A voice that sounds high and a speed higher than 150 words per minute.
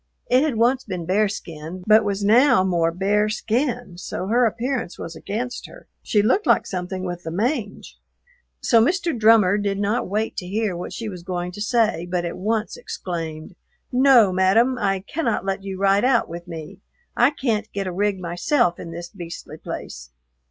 Yes: high, 200 Hz; average, 180 wpm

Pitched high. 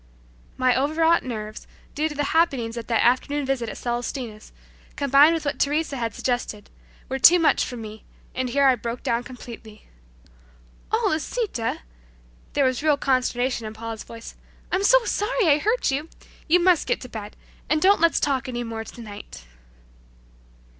Yes: very high, 260 Hz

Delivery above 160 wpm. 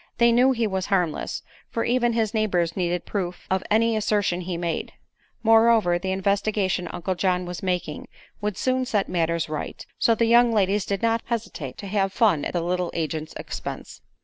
Yes: average, 180 wpm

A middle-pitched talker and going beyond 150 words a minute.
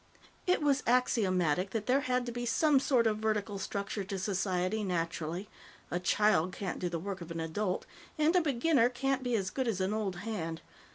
No: high, 210 Hz; average, 195 wpm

